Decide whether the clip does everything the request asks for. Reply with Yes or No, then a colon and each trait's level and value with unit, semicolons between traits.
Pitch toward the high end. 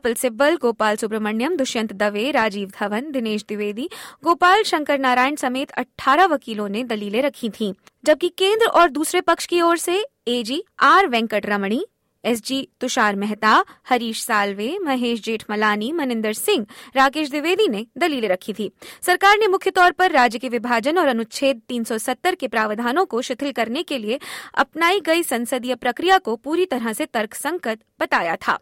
Yes: very high, 255 Hz